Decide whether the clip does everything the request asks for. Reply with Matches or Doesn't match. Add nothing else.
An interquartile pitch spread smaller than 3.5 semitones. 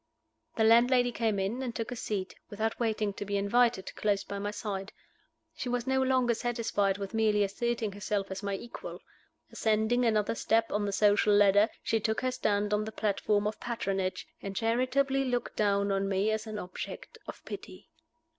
Matches